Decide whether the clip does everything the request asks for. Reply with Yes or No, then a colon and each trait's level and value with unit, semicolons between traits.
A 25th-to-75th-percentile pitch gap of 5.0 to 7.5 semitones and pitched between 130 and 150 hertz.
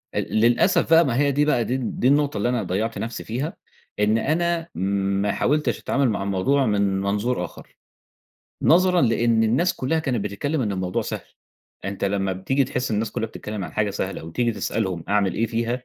No: average, 5.3 semitones; low, 115 Hz